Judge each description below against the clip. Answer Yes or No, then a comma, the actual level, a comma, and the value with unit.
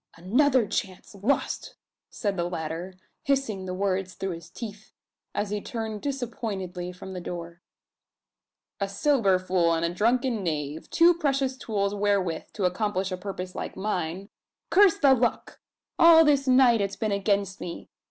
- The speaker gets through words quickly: No, average, 150 wpm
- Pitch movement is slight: No, average, 4.9 semitones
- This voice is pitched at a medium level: No, high, 200 Hz